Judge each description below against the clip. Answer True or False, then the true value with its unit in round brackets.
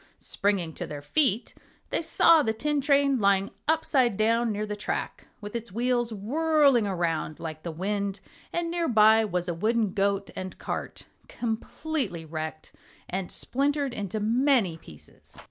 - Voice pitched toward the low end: False (215 Hz)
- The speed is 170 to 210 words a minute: False (150 wpm)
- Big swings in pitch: True (5.9 semitones)